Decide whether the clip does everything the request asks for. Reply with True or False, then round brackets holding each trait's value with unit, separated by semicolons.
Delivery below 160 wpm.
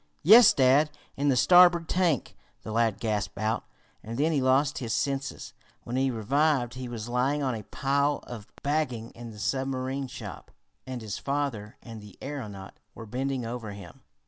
False (170 wpm)